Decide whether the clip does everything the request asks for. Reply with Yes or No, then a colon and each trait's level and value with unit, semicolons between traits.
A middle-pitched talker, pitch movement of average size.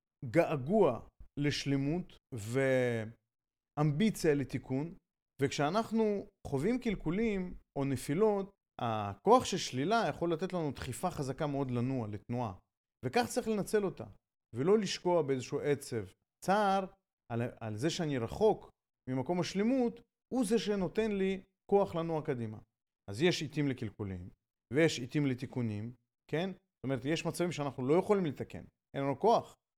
No: medium, 150 Hz; wide, 7.0 semitones